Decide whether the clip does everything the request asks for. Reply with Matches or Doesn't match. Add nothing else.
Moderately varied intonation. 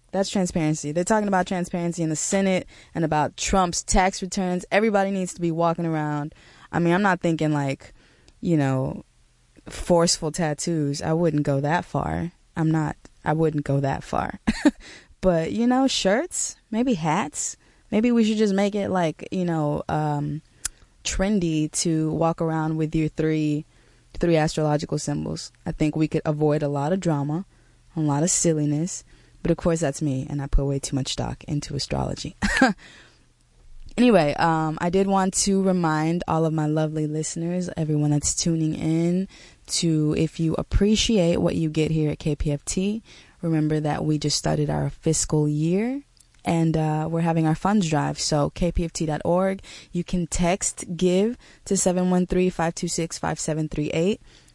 Matches